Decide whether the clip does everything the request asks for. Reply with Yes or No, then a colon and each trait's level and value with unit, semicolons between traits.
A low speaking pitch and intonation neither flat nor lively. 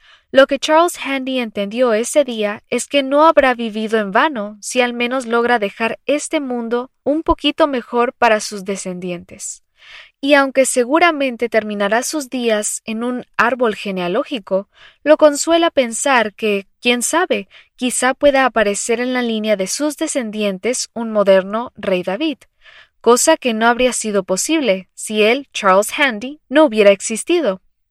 No: high, 245 Hz; average, 4.8 semitones